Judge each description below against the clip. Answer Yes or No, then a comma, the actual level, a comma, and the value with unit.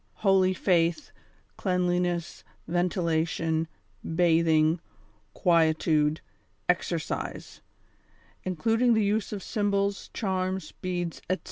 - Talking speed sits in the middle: No, slow, 80 wpm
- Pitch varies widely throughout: No, average, 2.7 semitones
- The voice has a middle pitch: Yes, medium, 180 Hz